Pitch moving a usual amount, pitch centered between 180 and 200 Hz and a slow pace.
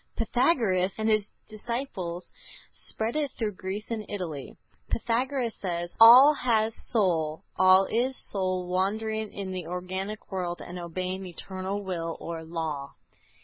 Yes: average, 3.7 semitones; high, 190 Hz; slow, 130 wpm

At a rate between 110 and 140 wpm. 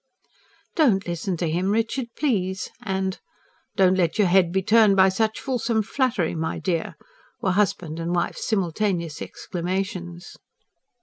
Yes: slow, 135 wpm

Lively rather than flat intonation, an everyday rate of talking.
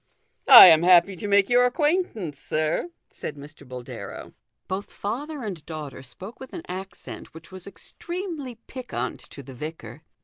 Yes: wide, 8.0 semitones; average, 160 wpm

